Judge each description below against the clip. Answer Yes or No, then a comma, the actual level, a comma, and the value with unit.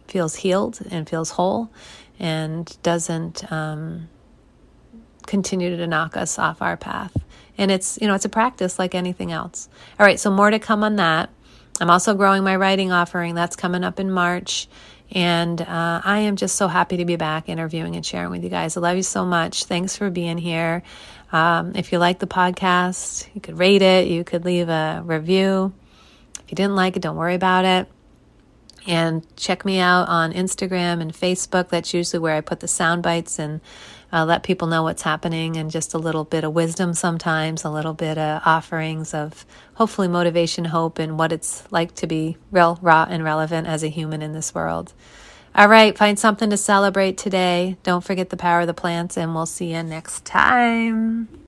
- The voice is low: No, medium, 175 Hz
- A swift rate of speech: No, average, 195 wpm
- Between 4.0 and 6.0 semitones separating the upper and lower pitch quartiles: No, narrow, 2.5 semitones